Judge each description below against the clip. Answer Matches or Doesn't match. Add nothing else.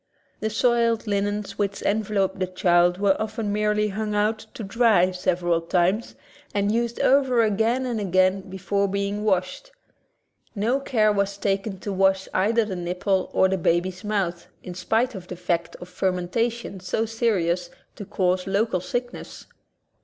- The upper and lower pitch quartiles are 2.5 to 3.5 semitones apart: Matches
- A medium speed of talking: Matches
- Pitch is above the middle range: Matches